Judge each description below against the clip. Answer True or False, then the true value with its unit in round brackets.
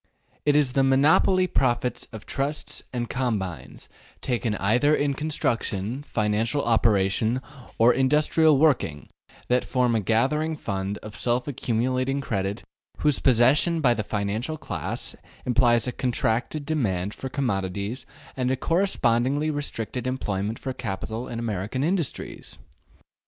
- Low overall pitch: True (125 Hz)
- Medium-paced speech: False (125 wpm)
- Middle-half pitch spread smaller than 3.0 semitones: False (4.4 semitones)